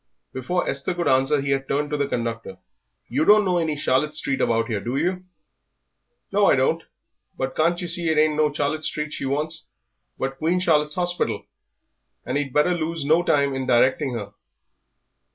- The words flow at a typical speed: Yes, average, 190 wpm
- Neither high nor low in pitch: Yes, medium, 150 Hz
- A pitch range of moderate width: Yes, average, 3.5 semitones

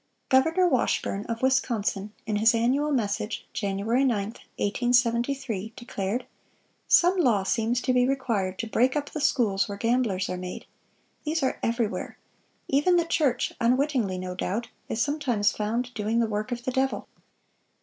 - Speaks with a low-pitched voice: No, high, 235 Hz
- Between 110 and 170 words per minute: Yes, average, 150 wpm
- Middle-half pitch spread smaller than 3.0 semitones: No, average, 4.1 semitones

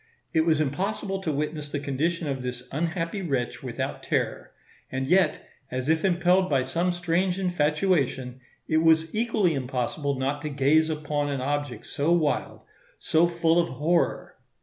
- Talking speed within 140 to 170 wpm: Yes, average, 155 wpm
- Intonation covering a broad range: No, average, 3.6 semitones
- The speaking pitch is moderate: Yes, medium, 155 Hz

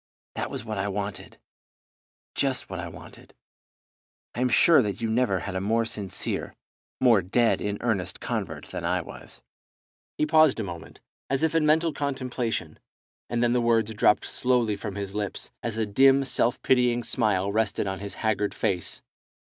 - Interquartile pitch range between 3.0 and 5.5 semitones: Yes, average, 3.9 semitones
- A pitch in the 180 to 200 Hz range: No, low, 110 Hz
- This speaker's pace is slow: No, average, 170 wpm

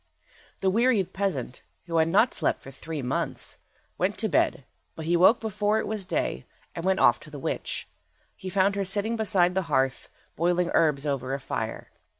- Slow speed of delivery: No, average, 185 wpm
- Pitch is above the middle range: No, medium, 180 Hz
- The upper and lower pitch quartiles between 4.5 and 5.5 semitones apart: Yes, average, 4.8 semitones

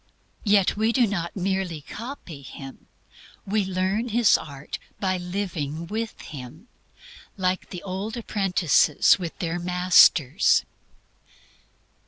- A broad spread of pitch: No, average, 3.5 semitones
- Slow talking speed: Yes, slow, 110 wpm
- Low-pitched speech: No, medium, 185 Hz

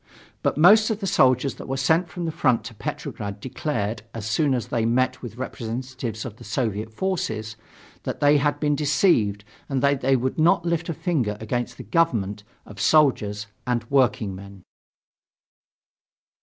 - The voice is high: No, low, 130 Hz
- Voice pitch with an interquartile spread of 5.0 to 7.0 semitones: Yes, wide, 5.4 semitones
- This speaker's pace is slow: No, average, 165 wpm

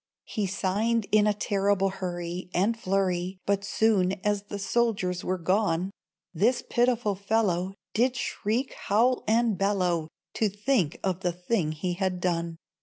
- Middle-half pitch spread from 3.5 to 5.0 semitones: No, average, 3.1 semitones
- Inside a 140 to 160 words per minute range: Yes, average, 145 wpm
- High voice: Yes, high, 195 Hz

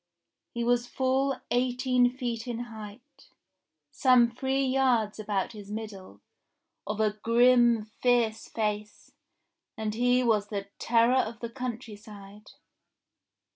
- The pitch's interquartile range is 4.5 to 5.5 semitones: No, average, 2.8 semitones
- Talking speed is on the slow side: Yes, slow, 125 wpm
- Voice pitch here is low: No, high, 235 Hz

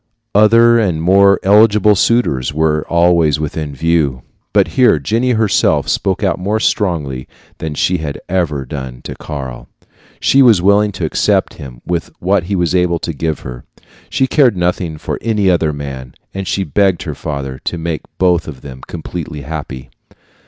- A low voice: Yes, very low, 85 Hz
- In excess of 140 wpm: Yes, average, 165 wpm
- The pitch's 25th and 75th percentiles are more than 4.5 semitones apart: Yes, average, 5.2 semitones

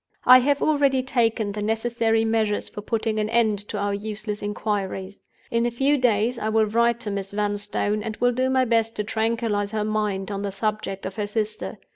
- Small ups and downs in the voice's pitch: Yes, narrow, 2.2 semitones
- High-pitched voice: Yes, high, 220 Hz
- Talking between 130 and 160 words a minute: No, average, 200 wpm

